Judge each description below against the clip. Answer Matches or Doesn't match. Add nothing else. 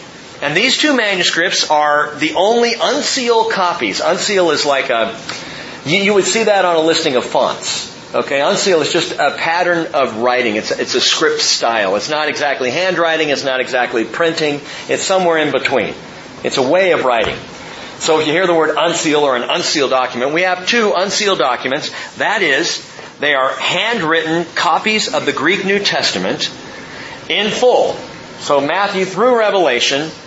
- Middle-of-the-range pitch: Matches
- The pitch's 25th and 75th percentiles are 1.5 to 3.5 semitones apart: Doesn't match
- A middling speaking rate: Matches